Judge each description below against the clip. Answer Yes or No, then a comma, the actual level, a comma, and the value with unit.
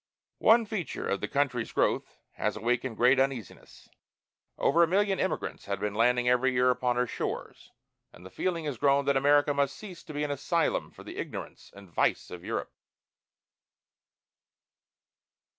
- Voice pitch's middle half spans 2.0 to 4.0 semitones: Yes, average, 3.5 semitones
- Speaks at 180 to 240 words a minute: No, average, 160 wpm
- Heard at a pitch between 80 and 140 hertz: Yes, low, 135 Hz